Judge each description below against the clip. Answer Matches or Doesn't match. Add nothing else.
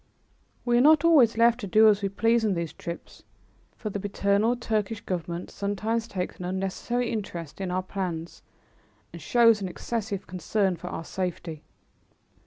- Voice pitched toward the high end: Matches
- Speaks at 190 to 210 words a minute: Doesn't match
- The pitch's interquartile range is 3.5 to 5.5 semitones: Matches